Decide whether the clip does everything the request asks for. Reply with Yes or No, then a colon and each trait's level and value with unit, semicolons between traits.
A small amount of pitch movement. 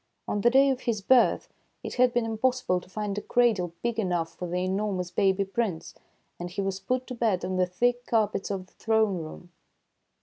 No: average, 4.5 semitones